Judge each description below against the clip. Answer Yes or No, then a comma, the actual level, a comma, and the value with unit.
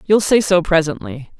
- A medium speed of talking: Yes, average, 170 wpm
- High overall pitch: No, medium, 165 Hz